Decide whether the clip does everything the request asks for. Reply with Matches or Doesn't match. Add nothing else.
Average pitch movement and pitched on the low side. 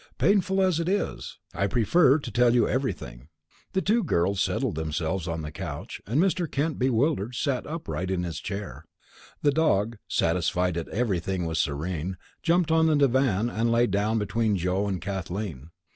Doesn't match